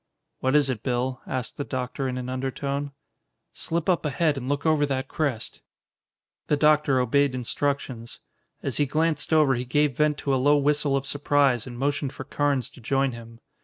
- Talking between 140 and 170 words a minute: No, average, 185 wpm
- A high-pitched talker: No, medium, 140 Hz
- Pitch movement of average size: No, narrow, 2.3 semitones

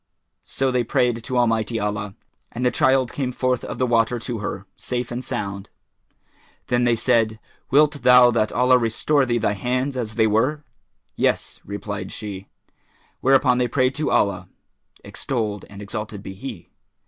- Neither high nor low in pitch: No, low, 120 Hz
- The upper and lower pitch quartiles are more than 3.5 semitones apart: No, average, 2.9 semitones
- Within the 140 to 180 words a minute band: Yes, average, 160 wpm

